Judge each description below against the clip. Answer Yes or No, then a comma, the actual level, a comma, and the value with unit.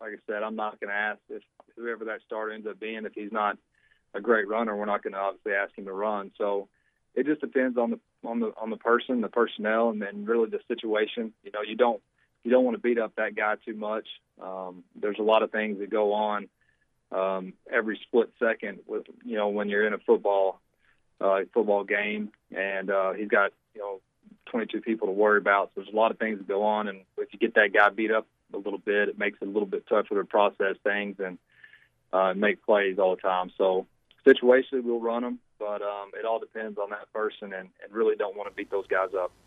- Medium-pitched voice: No, low, 105 Hz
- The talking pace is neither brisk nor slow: No, fast, 240 wpm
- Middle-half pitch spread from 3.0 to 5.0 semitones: No, narrow, 2.5 semitones